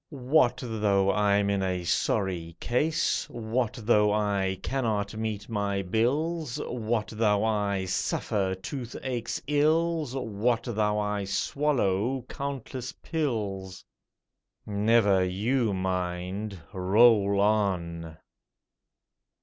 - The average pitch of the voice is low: Yes, low, 105 Hz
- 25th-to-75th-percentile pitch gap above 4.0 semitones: No, average, 3.7 semitones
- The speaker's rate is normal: No, slow, 95 wpm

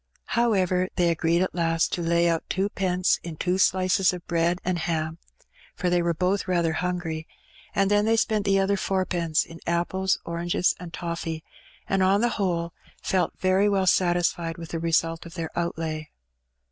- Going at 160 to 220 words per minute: Yes, average, 170 wpm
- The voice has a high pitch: No, medium, 175 Hz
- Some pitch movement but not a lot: No, narrow, 2.1 semitones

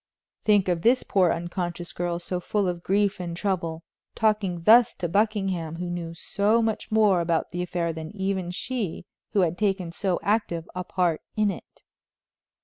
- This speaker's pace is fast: No, average, 170 wpm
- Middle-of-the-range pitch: Yes, medium, 180 Hz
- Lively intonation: No, average, 3.2 semitones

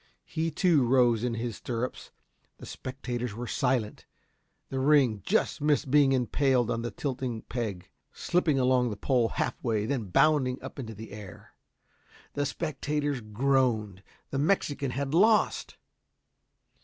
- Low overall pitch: Yes, low, 130 Hz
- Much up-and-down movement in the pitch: No, average, 3.6 semitones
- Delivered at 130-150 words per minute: Yes, average, 140 wpm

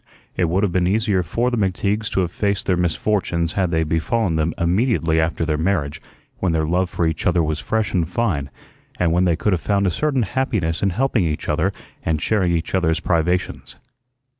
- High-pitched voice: No, very low, 90 Hz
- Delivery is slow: No, fast, 205 wpm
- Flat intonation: No, average, 3.7 semitones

